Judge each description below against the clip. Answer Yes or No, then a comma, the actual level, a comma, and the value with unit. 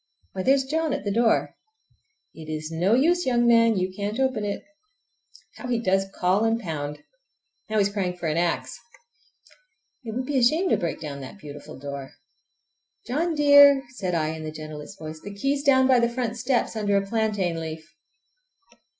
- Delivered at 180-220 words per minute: Yes, average, 185 wpm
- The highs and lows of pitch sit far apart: Yes, wide, 7.5 semitones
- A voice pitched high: Yes, high, 205 Hz